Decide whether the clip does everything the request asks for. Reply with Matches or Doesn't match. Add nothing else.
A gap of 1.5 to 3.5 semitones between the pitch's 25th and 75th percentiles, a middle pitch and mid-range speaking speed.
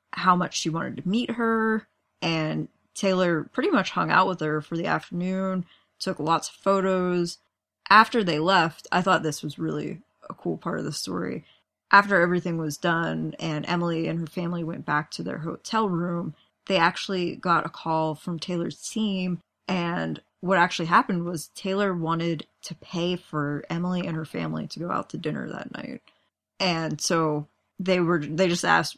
Matches